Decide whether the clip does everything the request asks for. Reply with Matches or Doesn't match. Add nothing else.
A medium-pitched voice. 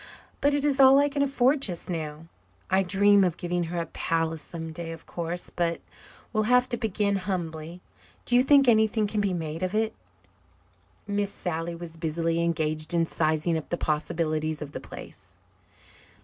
Matches